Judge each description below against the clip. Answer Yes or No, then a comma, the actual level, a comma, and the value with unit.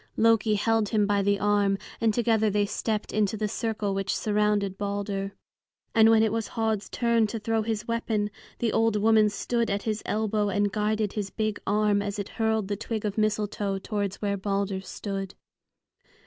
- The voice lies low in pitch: No, high, 210 Hz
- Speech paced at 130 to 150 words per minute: No, average, 180 wpm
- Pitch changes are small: Yes, narrow, 1.5 semitones